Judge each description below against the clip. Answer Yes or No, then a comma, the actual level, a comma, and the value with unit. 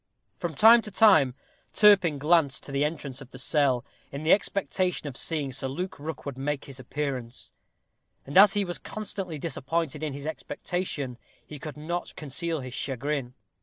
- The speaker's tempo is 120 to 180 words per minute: Yes, average, 165 wpm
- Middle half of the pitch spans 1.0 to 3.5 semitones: No, average, 4.2 semitones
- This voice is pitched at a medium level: Yes, medium, 150 Hz